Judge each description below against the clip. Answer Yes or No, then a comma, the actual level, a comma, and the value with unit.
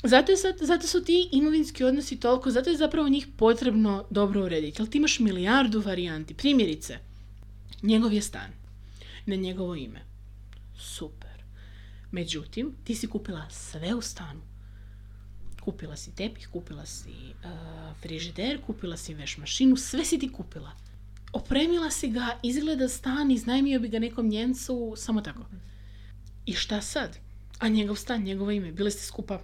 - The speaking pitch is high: Yes, high, 200 Hz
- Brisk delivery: No, average, 150 wpm